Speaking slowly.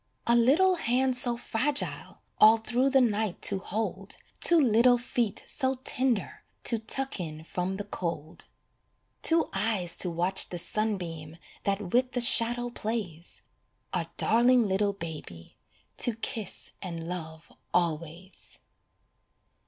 Yes: slow, 130 wpm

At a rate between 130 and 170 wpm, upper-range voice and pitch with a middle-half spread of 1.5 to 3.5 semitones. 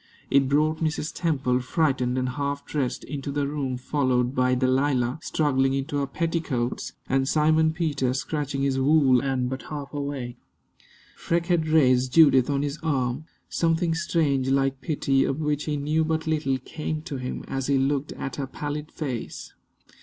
No: average, 165 wpm; medium, 140 Hz; average, 2.7 semitones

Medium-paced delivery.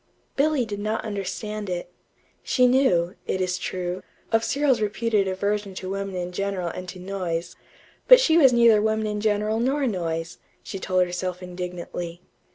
Yes: average, 165 wpm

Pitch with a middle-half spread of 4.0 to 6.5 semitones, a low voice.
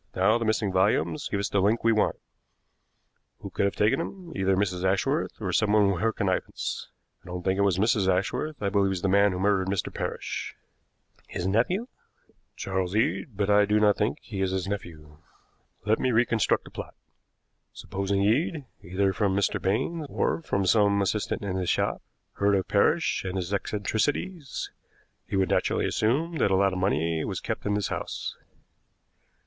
No: narrow, 2.6 semitones; low, 100 Hz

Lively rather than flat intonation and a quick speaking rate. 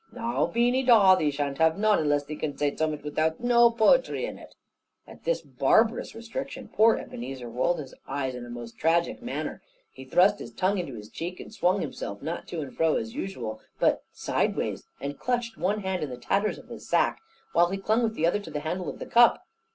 Yes: wide, 7.6 semitones; fast, 215 wpm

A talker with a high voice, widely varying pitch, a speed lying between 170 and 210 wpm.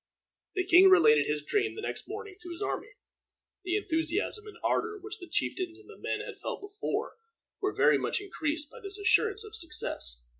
No: very high, 380 Hz; average, 3.8 semitones; average, 190 wpm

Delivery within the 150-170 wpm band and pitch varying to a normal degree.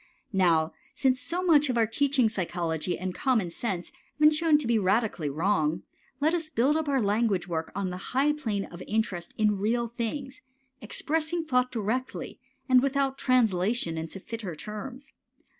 No: average, 160 wpm; wide, 6.5 semitones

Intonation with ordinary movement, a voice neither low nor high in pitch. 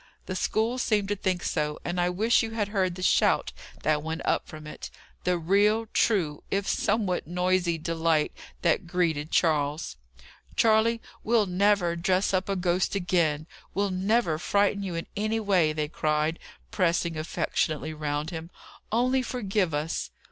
Yes: average, 4.2 semitones; medium, 180 Hz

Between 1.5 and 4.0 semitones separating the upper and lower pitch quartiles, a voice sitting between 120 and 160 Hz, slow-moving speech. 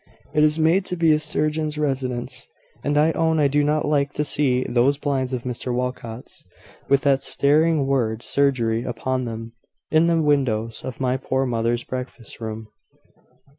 No: average, 3.5 semitones; low, 135 Hz; average, 170 wpm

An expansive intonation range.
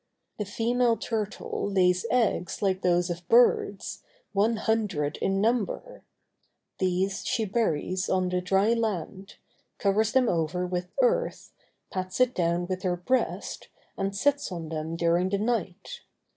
No: average, 4.0 semitones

